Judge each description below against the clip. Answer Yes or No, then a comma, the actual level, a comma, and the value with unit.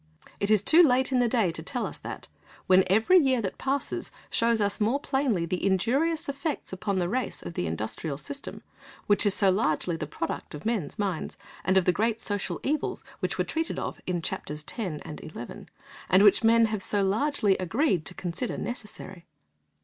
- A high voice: Yes, high, 205 Hz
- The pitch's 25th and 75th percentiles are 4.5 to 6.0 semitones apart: Yes, wide, 5.6 semitones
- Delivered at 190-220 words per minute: Yes, average, 195 wpm